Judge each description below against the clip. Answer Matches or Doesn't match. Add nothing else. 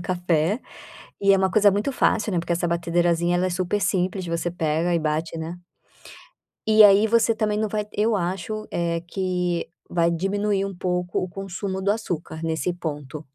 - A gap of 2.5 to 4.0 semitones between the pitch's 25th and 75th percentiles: Matches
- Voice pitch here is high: Doesn't match